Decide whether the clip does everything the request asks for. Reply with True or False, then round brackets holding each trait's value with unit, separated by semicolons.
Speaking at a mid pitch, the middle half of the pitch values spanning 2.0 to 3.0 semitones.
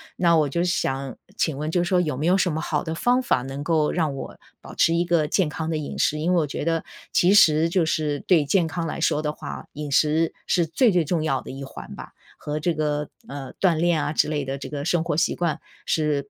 True (155 Hz; 2.5 semitones)